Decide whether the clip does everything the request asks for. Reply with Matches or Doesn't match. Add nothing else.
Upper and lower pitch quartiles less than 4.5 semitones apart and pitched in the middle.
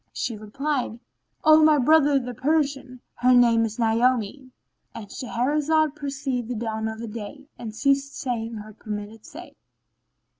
Doesn't match